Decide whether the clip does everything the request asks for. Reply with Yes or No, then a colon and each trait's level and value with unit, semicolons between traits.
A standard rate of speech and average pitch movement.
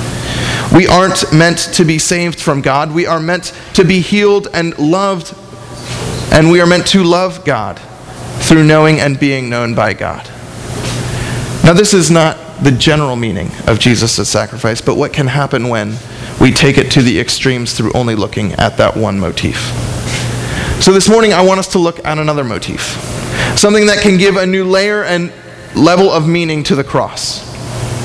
No: average, 180 wpm; wide, 6.9 semitones